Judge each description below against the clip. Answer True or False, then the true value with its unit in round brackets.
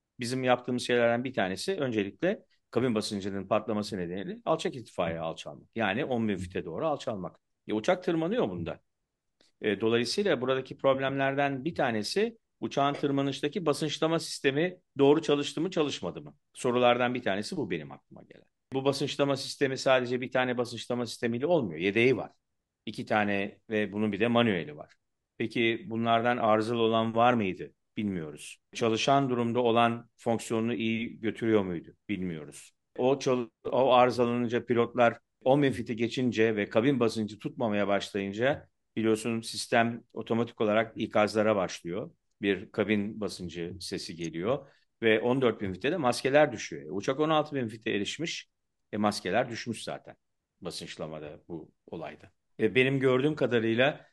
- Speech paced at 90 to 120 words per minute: False (135 wpm)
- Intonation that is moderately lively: True (3.6 semitones)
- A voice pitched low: True (120 Hz)